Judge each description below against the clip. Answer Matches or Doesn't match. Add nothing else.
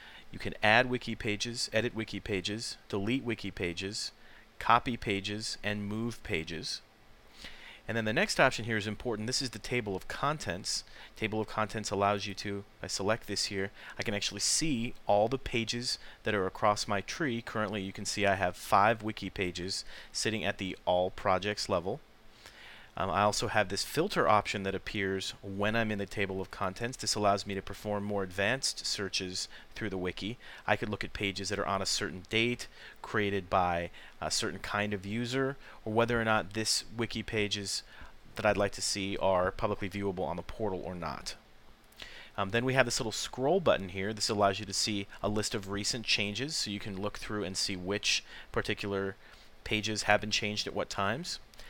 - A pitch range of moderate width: Doesn't match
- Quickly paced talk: Doesn't match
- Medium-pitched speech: Doesn't match